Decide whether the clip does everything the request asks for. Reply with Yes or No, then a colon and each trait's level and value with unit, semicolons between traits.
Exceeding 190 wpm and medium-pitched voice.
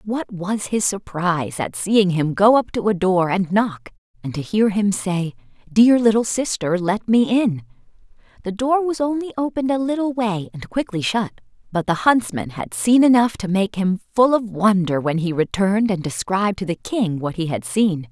No: average, 200 wpm; high, 200 Hz